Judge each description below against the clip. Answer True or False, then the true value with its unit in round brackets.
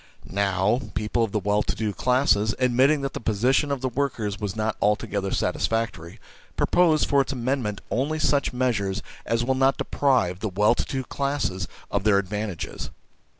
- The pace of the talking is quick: False (170 wpm)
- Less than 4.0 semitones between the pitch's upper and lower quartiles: False (4.5 semitones)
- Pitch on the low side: True (115 Hz)